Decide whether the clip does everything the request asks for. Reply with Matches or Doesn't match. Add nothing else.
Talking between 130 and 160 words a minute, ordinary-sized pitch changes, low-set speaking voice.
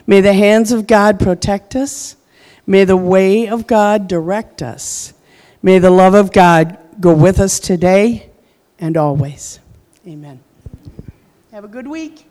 Doesn't match